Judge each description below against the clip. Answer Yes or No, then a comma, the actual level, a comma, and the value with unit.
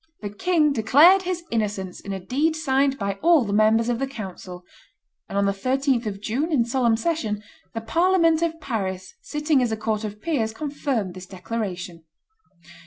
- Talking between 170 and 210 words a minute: Yes, average, 175 wpm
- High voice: Yes, high, 230 Hz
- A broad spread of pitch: Yes, wide, 6.7 semitones